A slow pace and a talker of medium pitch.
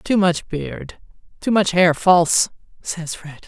Yes: slow, 120 wpm; medium, 175 Hz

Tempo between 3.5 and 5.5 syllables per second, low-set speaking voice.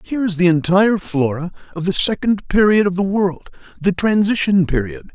No: 5.4 syllables/s; medium, 185 Hz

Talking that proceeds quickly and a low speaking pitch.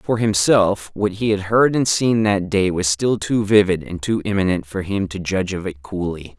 Yes: fast, 225 wpm; low, 100 Hz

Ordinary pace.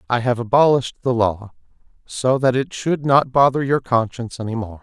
Yes: average, 185 wpm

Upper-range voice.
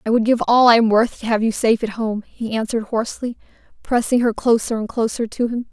Yes: high, 230 Hz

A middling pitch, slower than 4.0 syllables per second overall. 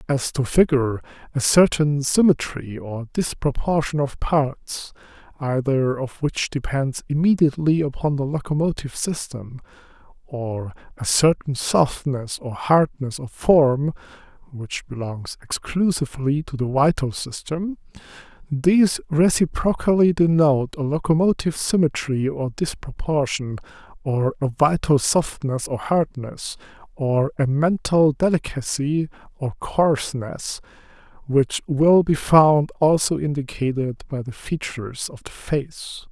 Yes: medium, 145 Hz; 3.2 syllables/s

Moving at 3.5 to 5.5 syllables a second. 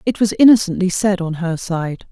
Yes: 5.1 syllables/s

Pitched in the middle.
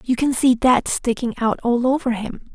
No: high, 245 Hz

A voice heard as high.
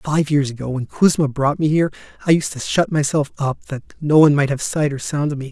No: medium, 145 Hz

